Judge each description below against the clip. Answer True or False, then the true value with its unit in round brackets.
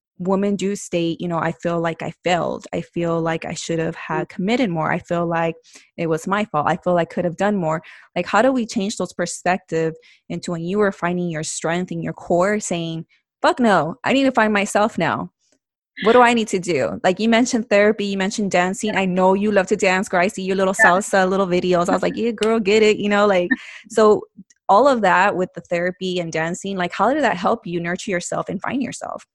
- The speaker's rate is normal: False (240 wpm)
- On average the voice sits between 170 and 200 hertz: True (185 Hz)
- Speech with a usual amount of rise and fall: True (3.2 semitones)